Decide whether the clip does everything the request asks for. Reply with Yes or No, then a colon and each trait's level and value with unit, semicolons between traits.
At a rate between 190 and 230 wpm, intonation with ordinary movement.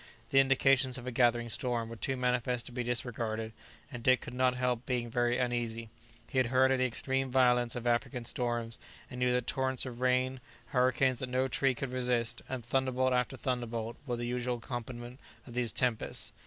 No: average, 195 wpm; narrow, 1.3 semitones